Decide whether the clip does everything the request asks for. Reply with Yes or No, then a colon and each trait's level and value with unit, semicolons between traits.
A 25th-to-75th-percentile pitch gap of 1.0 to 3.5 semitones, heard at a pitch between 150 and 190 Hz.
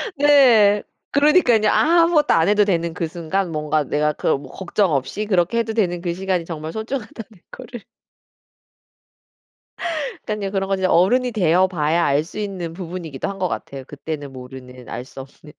No: average, 5.3 semitones; medium, 185 Hz